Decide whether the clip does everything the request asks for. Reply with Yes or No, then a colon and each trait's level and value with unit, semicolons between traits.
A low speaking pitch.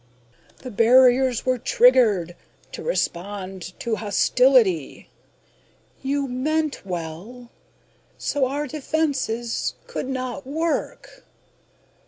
No: very high, 250 Hz